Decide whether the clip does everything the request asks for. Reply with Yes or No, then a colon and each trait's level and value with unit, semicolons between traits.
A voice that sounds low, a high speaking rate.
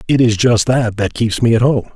Yes: low, 115 Hz; fast, 275 wpm